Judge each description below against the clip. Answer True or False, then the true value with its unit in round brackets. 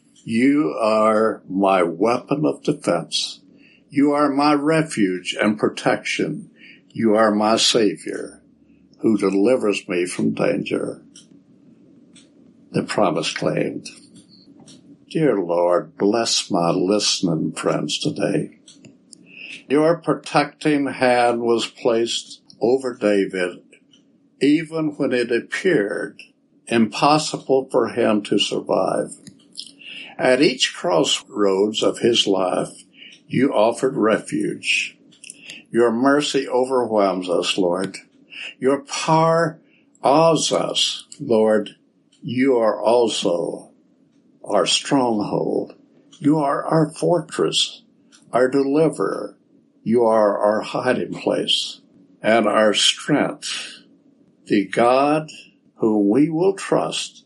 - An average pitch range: False (5.8 semitones)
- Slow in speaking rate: True (95 wpm)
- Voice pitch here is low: True (125 Hz)